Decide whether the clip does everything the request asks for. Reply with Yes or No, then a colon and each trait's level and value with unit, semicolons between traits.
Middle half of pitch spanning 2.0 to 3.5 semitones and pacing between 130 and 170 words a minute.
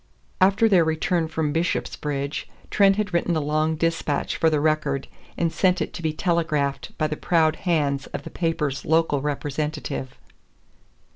Yes: narrow, 2.5 semitones; average, 155 wpm